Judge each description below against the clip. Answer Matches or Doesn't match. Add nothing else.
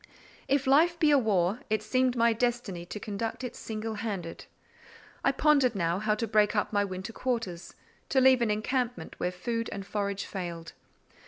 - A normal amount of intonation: Matches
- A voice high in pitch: Matches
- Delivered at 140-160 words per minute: Doesn't match